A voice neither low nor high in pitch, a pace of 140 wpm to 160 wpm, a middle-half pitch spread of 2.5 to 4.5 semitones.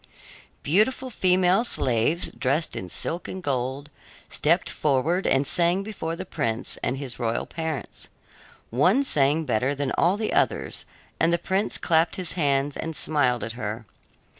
No: medium, 155 Hz; average, 150 wpm; average, 5.2 semitones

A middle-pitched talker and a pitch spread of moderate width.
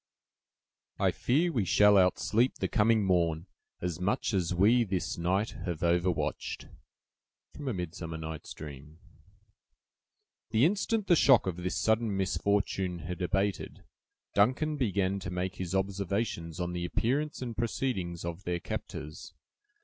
No: very low, 95 Hz; average, 4.3 semitones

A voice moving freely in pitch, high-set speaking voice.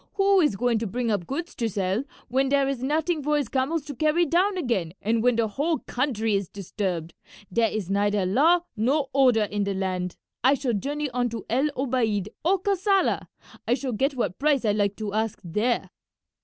Yes: wide, 5.7 semitones; high, 245 Hz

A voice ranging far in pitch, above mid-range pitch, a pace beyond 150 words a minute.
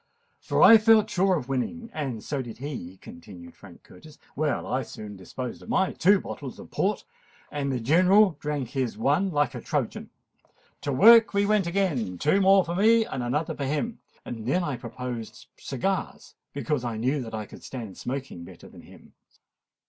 No: wide, 7.7 semitones; medium, 140 Hz; average, 175 wpm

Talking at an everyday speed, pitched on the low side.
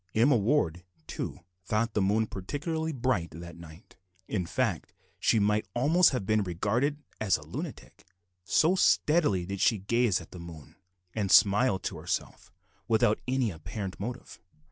Yes: average, 150 wpm; low, 105 Hz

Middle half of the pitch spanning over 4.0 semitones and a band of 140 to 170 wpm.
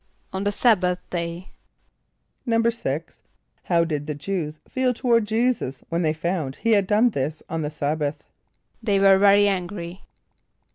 Yes: average, 4.9 semitones; average, 150 wpm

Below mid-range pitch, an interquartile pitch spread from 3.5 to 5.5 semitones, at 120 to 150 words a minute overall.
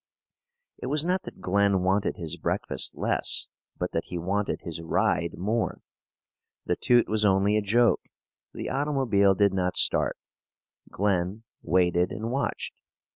Yes: low, 100 Hz; average, 3.9 semitones; average, 140 wpm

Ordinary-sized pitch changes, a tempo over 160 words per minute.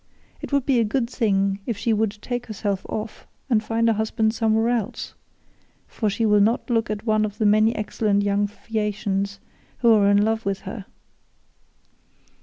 No: narrow, 1.8 semitones; average, 180 wpm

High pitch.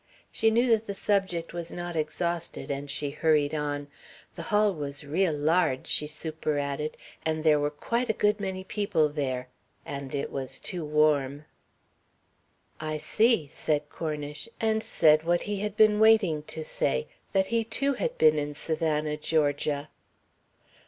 No: medium, 155 Hz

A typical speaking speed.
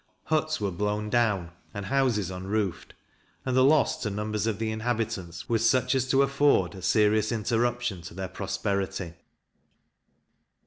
Yes: average, 145 wpm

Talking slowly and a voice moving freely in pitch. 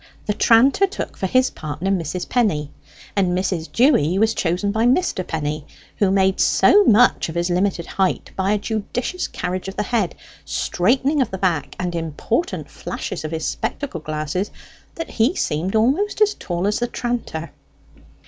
No: average, 165 wpm; wide, 5.7 semitones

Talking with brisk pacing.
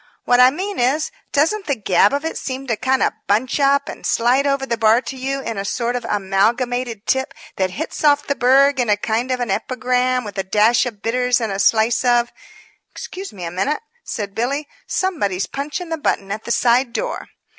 Yes: fast, 215 wpm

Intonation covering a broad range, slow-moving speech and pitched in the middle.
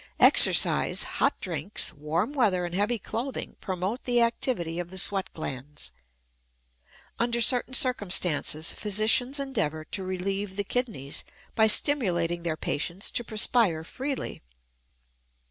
No: wide, 5.8 semitones; slow, 120 wpm; high, 195 Hz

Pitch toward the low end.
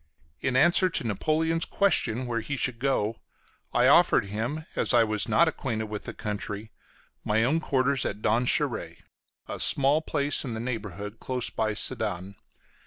Yes: low, 120 Hz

